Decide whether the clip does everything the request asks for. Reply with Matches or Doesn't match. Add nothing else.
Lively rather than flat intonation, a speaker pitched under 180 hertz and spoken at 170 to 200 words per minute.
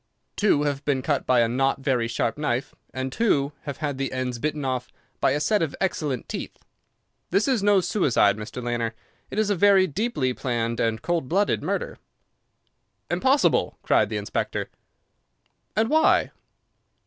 Doesn't match